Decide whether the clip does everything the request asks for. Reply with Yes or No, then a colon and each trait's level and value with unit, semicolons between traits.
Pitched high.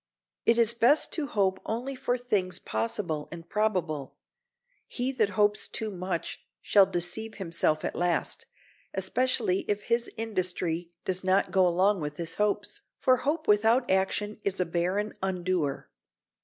Yes: high, 195 Hz